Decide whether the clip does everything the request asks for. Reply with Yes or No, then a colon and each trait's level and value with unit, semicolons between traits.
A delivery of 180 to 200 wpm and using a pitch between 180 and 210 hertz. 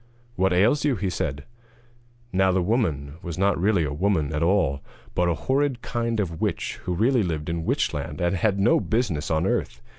No: average, 190 wpm; very low, 95 Hz